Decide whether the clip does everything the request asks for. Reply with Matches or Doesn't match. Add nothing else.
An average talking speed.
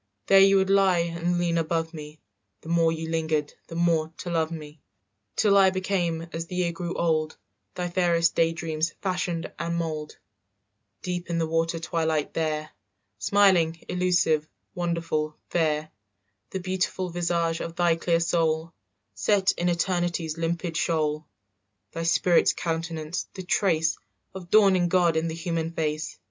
Matches